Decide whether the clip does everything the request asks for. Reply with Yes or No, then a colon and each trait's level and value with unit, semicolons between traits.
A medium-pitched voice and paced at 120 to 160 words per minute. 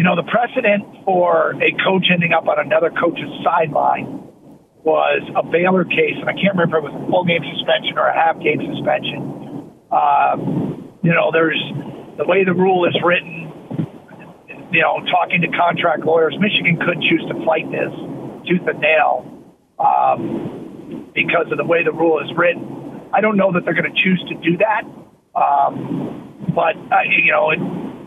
No: medium, 175 Hz; average, 180 wpm